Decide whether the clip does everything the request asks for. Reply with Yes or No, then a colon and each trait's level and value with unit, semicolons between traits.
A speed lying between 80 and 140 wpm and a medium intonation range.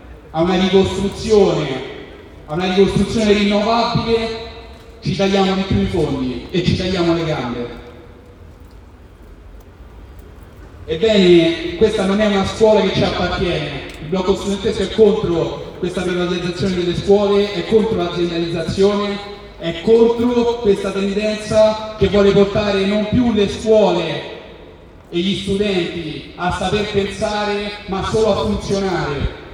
Yes: average, 120 wpm; average, 3.8 semitones